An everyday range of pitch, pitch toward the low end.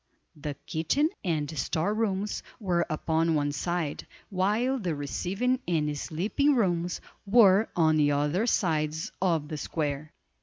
No: average, 4.8 semitones; medium, 170 Hz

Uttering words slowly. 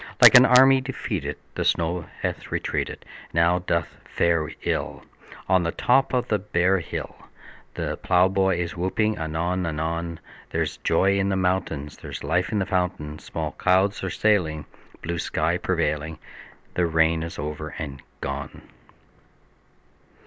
No: average, 145 wpm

